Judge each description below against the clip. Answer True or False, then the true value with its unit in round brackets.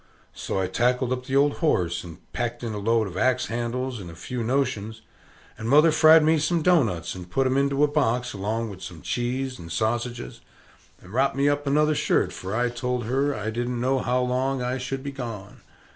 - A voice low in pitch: True (125 Hz)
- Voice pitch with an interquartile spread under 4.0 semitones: True (3.5 semitones)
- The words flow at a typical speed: False (210 wpm)